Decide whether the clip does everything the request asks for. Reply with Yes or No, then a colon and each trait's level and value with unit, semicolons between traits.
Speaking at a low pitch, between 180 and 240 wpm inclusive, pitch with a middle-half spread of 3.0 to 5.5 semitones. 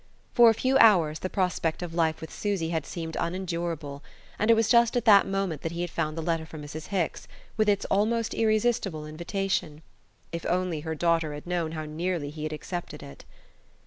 No: medium, 170 Hz; average, 200 wpm; average, 3.9 semitones